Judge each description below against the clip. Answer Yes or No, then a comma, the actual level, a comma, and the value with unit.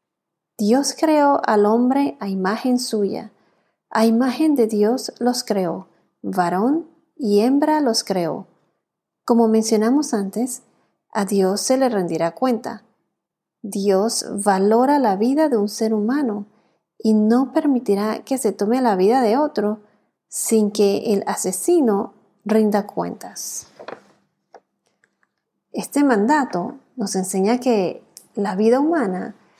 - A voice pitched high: Yes, high, 220 Hz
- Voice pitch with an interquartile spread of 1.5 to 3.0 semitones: No, average, 3.7 semitones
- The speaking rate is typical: No, slow, 120 wpm